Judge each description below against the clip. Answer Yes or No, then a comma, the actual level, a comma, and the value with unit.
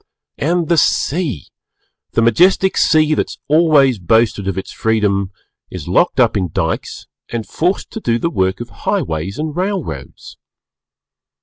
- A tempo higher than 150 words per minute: No, average, 145 wpm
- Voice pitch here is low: Yes, low, 125 Hz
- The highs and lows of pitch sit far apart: Yes, wide, 8.9 semitones